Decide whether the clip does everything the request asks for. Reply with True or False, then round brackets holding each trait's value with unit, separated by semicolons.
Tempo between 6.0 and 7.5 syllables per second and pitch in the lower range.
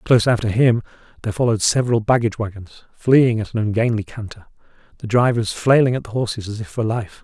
True (6.4 syllables/s; 110 Hz)